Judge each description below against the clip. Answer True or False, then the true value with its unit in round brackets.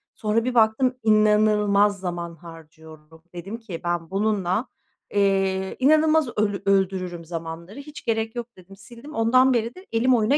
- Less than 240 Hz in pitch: True (210 Hz)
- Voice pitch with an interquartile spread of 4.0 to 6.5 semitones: True (4.7 semitones)